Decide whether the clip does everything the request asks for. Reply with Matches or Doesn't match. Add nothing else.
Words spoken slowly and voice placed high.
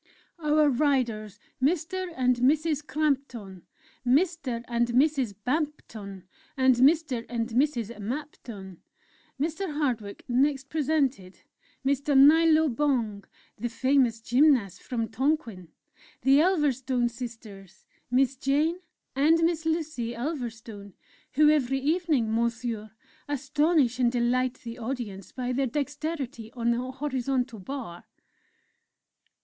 Matches